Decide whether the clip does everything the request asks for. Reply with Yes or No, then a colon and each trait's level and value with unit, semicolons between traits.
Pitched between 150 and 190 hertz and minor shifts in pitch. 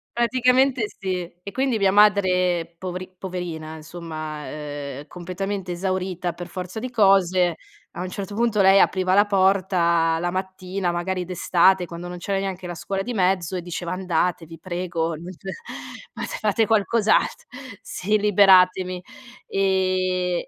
Yes: medium, 185 Hz; narrow, 2.1 semitones